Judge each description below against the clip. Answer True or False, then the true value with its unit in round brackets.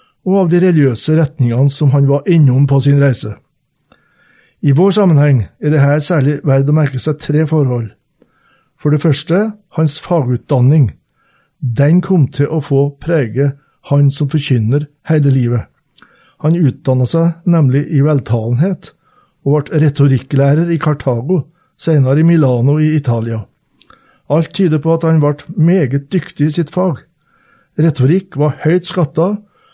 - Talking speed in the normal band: True (145 wpm)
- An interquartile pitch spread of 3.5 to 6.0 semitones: False (3.1 semitones)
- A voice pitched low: False (150 Hz)